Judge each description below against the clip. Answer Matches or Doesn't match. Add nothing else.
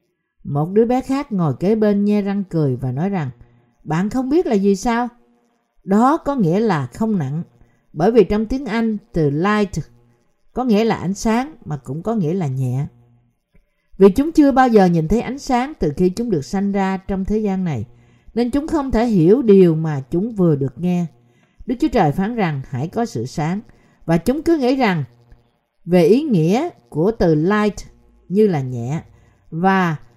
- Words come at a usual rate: Matches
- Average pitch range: Doesn't match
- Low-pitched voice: Doesn't match